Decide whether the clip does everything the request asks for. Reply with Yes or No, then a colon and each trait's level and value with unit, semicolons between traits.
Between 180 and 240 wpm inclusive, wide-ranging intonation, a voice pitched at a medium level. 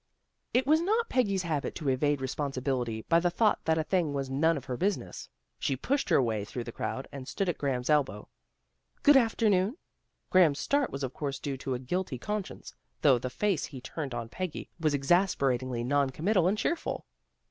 Yes: average, 200 wpm; wide, 6.3 semitones; medium, 150 Hz